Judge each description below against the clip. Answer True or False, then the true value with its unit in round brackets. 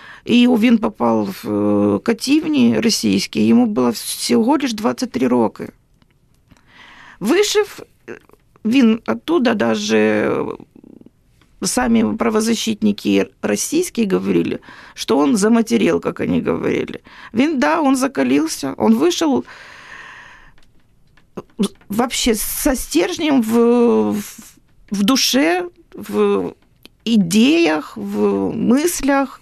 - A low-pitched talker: False (230 Hz)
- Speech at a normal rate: False (90 wpm)